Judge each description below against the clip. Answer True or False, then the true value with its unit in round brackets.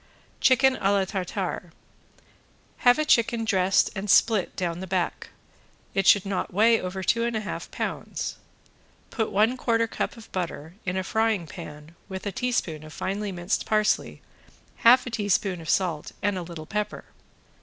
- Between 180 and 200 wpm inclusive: False (165 wpm)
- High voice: True (195 Hz)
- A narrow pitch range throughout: False (3.8 semitones)